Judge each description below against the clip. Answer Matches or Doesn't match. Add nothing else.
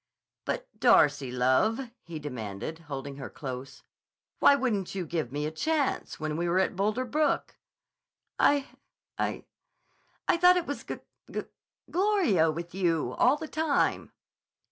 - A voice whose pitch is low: Doesn't match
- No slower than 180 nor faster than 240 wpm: Doesn't match